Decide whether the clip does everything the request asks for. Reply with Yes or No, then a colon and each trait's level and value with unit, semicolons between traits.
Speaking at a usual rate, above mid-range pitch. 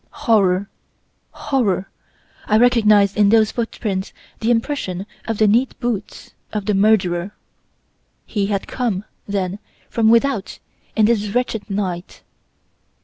No: slow, 120 wpm; high, 210 Hz